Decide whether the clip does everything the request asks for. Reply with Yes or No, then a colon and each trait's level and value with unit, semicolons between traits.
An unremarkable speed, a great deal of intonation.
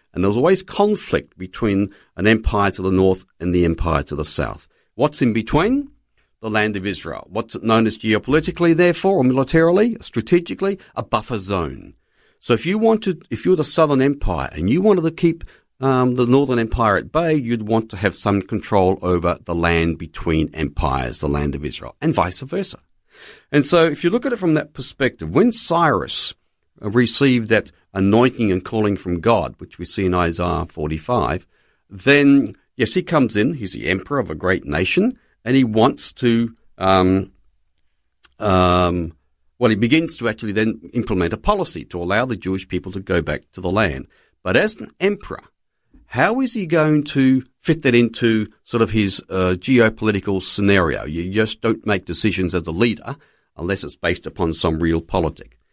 Yes: average, 180 wpm; wide, 7.1 semitones